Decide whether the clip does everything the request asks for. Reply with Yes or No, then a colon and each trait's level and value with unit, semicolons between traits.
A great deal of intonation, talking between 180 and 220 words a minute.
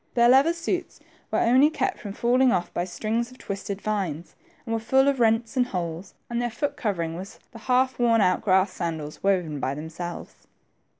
Yes: wide, 5.8 semitones; average, 190 wpm